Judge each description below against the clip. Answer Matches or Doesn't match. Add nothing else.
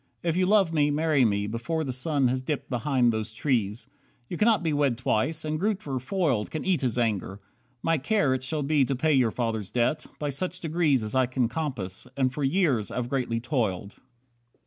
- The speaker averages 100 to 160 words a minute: Doesn't match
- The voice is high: Doesn't match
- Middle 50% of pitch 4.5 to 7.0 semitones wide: Matches